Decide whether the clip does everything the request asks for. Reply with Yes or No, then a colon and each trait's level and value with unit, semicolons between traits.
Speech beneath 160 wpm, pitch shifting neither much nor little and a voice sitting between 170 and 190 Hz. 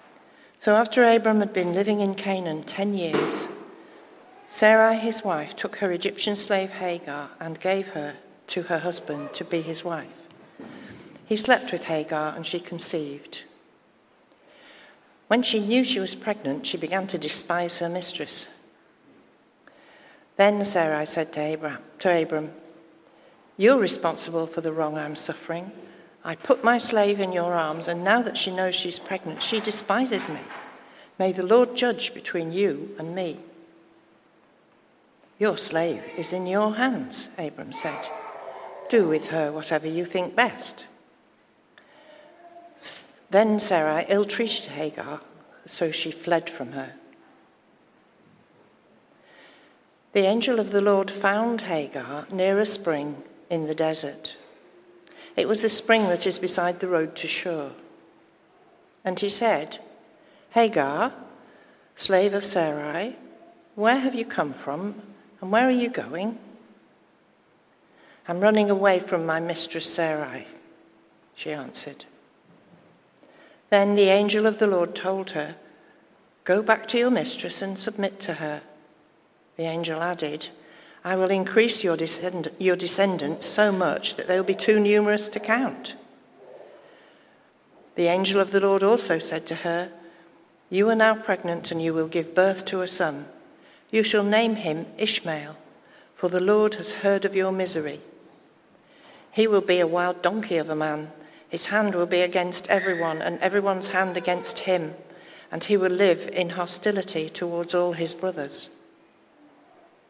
Yes: average, 140 wpm; average, 4.2 semitones; medium, 185 Hz